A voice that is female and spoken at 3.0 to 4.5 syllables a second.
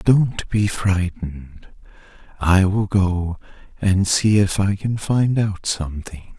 No: male; 3.4 syllables/s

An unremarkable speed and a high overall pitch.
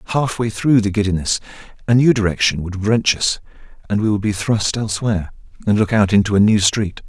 No: average, 195 wpm; low, 105 Hz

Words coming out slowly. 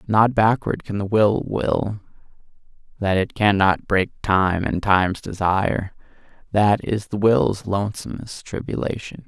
Yes: slow, 125 wpm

